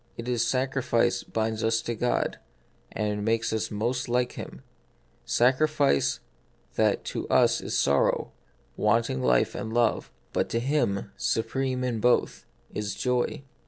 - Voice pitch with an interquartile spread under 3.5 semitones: Yes, average, 2.8 semitones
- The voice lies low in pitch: Yes, low, 115 Hz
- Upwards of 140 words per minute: No, slow, 135 wpm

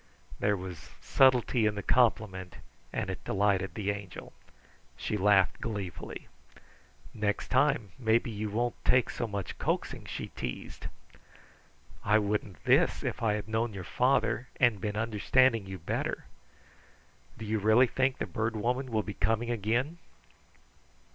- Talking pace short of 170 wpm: Yes, average, 140 wpm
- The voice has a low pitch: Yes, low, 110 Hz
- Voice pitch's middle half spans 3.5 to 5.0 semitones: No, average, 2.8 semitones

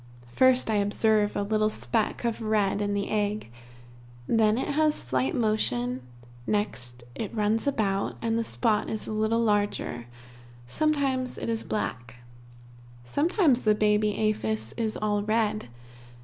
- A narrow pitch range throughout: Yes, narrow, 2.0 semitones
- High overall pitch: Yes, high, 215 Hz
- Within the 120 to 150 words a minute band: Yes, average, 140 wpm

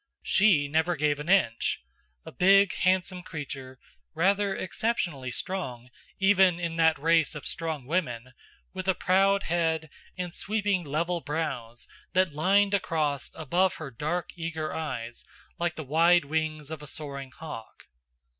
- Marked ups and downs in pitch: No, average, 4.2 semitones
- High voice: No, medium, 160 Hz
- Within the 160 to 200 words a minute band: No, average, 140 wpm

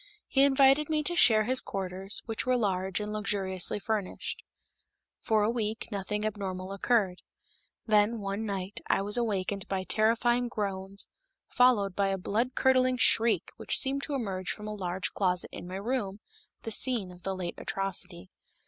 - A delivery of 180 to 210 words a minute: No, average, 165 wpm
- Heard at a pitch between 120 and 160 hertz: No, high, 210 Hz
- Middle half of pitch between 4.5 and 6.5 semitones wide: No, average, 3.6 semitones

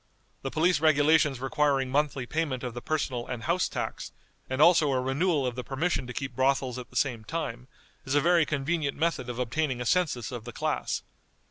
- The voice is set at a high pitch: No, low, 135 Hz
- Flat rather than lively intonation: No, average, 3.7 semitones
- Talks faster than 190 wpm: Yes, average, 200 wpm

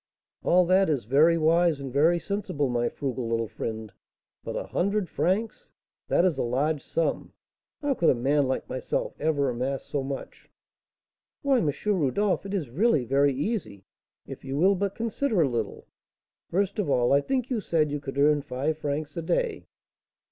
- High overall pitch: No, medium, 150 Hz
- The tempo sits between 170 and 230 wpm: Yes, average, 175 wpm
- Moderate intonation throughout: No, wide, 6.0 semitones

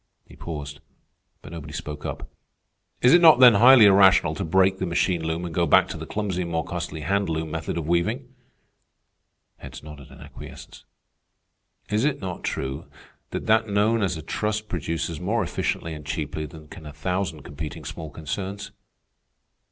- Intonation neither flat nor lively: Yes, average, 4.3 semitones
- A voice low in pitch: Yes, very low, 85 Hz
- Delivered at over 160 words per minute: Yes, average, 175 wpm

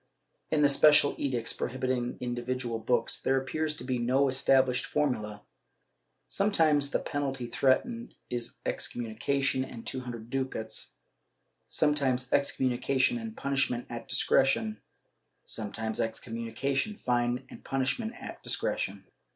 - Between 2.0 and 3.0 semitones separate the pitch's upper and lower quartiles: Yes, narrow, 2.6 semitones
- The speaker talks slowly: Yes, slow, 125 wpm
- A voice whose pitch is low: Yes, low, 130 Hz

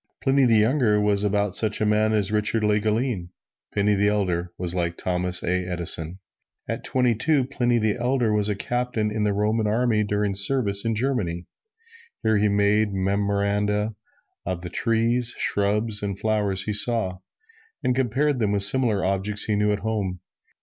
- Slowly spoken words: No, average, 170 wpm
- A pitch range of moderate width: No, narrow, 2.2 semitones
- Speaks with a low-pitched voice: Yes, low, 105 Hz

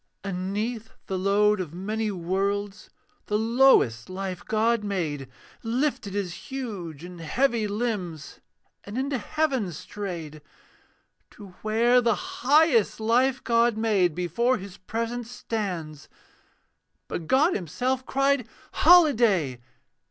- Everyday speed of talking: No, slow, 115 wpm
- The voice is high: Yes, high, 210 Hz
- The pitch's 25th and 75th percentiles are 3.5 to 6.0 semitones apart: Yes, average, 4.8 semitones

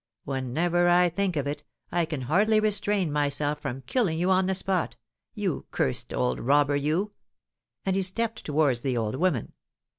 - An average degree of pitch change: Yes, average, 5.0 semitones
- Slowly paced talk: No, average, 170 wpm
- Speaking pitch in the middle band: Yes, medium, 160 Hz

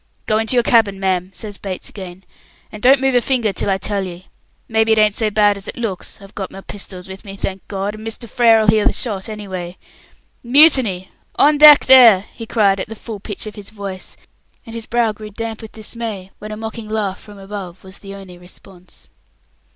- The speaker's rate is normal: No, fast, 215 wpm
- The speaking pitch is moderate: No, high, 210 Hz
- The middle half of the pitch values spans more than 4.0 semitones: No, narrow, 2.6 semitones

